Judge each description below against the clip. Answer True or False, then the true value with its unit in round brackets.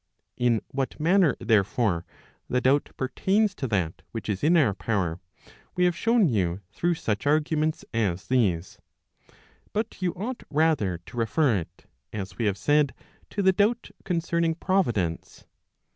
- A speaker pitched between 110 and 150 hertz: True (135 Hz)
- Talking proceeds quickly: False (145 wpm)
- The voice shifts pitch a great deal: True (8.8 semitones)